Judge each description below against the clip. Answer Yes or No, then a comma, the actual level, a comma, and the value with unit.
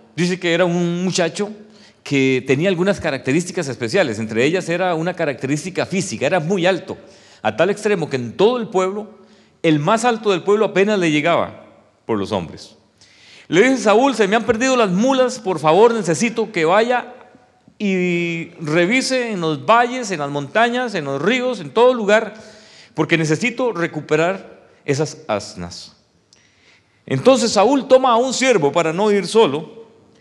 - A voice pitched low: No, high, 190 Hz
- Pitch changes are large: Yes, wide, 5.8 semitones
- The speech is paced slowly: No, average, 160 wpm